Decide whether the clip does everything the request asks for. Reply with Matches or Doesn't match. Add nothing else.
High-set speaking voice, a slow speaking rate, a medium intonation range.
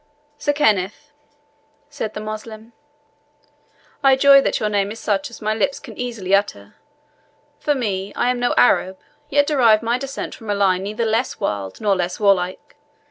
Doesn't match